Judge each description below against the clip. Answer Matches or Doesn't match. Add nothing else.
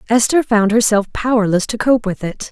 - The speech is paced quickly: Doesn't match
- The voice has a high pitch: Matches